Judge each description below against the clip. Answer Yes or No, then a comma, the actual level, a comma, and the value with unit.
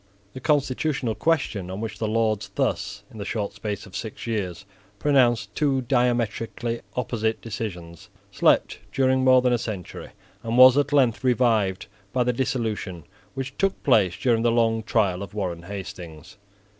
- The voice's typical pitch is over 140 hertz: No, low, 115 Hz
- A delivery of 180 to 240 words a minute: No, average, 155 wpm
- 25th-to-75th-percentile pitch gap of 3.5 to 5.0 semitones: Yes, average, 4.0 semitones